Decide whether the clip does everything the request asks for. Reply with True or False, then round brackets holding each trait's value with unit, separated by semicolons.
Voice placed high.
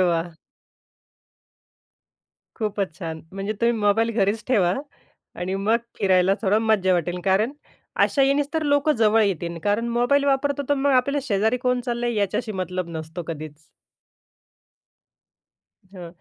True (210 Hz)